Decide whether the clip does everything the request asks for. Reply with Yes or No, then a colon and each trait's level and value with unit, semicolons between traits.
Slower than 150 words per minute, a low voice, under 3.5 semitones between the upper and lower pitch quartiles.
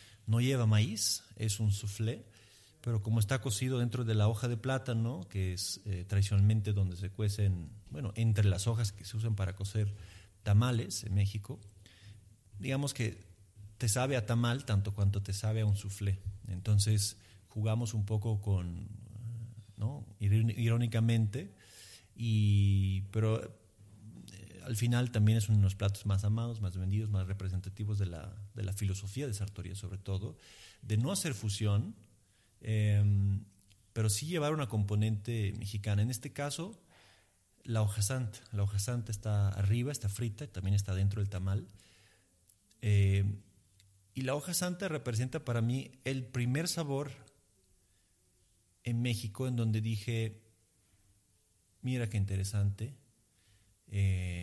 Yes: average, 140 wpm; low, 105 Hz; narrow, 2.5 semitones